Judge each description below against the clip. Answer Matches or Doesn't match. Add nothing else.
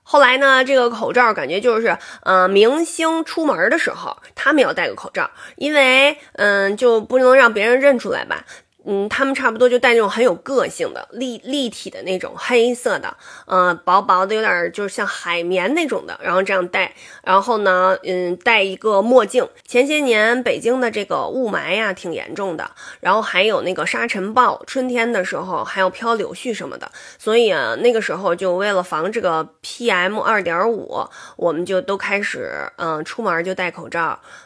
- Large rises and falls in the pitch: Matches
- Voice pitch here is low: Doesn't match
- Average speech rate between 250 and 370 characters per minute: Matches